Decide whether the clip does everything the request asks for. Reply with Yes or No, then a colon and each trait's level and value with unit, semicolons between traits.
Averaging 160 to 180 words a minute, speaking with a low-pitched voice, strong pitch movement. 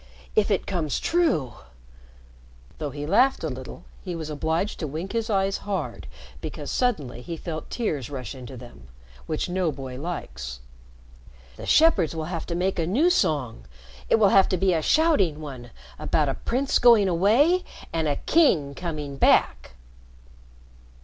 No: average, 165 wpm; medium, 160 Hz; wide, 6.4 semitones